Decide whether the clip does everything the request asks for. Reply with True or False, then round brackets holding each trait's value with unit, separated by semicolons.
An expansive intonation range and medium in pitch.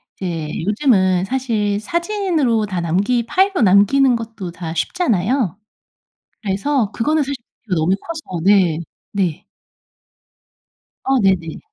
False (6.3 semitones; 210 Hz)